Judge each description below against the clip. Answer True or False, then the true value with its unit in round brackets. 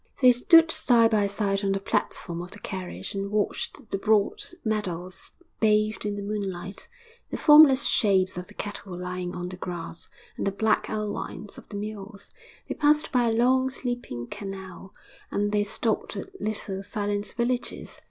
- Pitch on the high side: True (205 Hz)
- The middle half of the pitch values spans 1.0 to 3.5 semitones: True (2.8 semitones)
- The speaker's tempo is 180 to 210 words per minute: False (165 wpm)